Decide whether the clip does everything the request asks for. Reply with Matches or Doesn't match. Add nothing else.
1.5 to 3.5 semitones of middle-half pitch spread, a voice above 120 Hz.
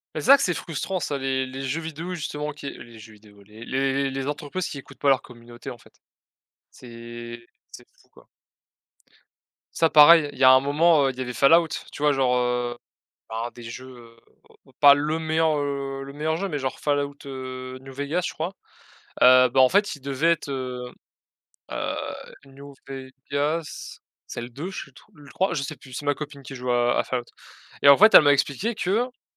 Matches